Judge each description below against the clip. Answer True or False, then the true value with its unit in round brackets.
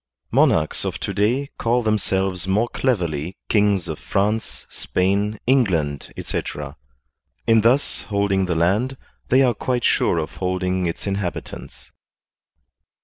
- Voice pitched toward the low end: True (100 Hz)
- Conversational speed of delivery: False (130 wpm)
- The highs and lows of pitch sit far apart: False (3.8 semitones)